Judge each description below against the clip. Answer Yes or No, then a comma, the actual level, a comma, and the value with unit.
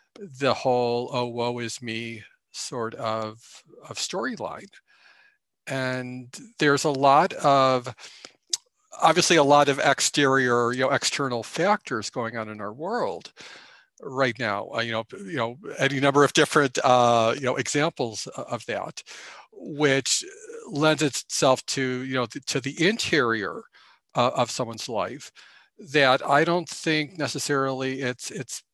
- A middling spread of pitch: Yes, average, 3.9 semitones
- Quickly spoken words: No, average, 140 wpm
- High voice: No, low, 135 Hz